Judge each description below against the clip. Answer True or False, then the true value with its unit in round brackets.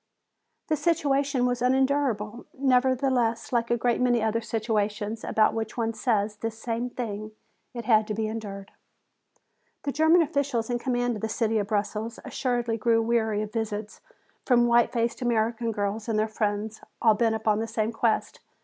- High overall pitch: True (230 Hz)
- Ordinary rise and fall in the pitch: False (2.2 semitones)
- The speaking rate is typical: True (165 wpm)